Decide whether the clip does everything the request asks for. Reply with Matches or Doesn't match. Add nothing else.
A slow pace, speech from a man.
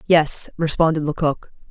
Doesn't match